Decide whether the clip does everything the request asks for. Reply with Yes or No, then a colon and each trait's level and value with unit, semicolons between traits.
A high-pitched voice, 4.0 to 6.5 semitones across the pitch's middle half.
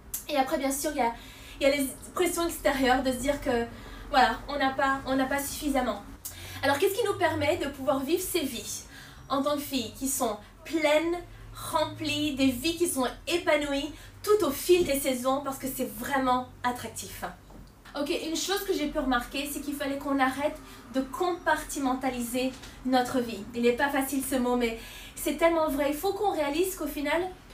No: very high, 280 Hz; average, 3.1 semitones